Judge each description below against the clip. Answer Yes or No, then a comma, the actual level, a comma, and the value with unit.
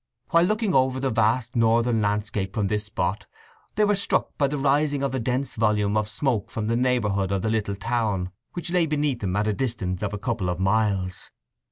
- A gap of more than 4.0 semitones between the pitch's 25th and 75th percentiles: Yes, average, 4.5 semitones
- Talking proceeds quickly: Yes, fast, 210 wpm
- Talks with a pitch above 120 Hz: No, low, 110 Hz